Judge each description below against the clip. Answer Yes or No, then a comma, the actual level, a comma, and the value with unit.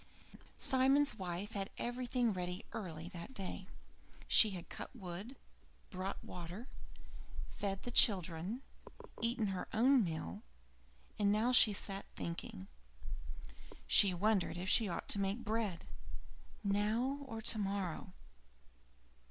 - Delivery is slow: Yes, slow, 120 wpm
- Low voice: No, high, 200 Hz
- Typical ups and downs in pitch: Yes, average, 4.1 semitones